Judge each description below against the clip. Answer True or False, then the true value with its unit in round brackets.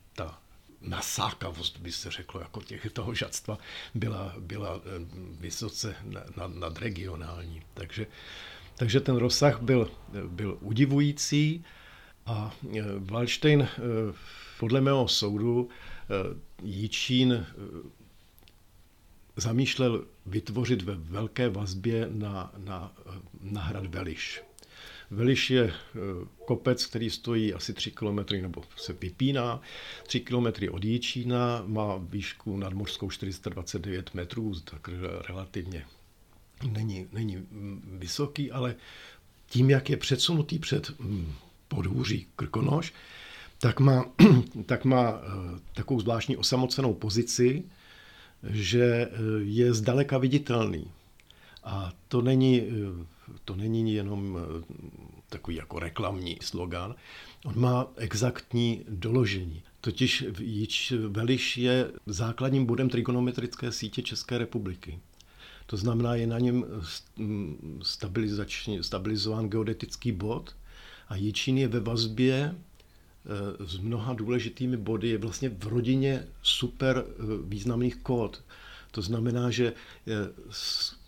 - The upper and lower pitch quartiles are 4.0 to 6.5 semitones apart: True (4.6 semitones)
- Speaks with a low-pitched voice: True (110 Hz)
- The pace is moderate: False (100 wpm)